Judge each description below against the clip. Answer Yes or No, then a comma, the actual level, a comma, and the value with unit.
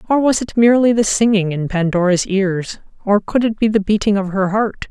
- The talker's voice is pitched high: Yes, high, 205 Hz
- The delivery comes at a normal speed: No, fast, 220 wpm